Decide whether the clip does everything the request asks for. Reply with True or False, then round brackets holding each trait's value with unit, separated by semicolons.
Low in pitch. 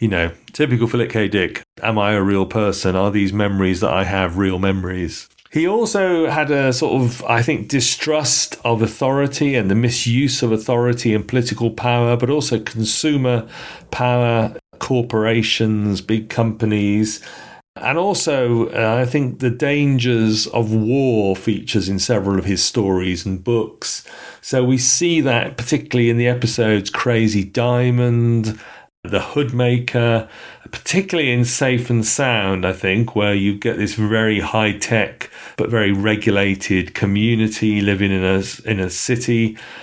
True (115 Hz)